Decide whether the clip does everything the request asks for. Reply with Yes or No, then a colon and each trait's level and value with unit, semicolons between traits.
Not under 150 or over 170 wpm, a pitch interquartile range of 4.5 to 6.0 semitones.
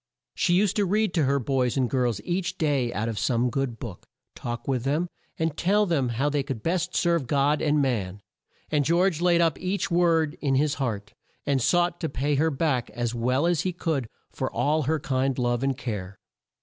No: fast, 205 wpm; average, 5.2 semitones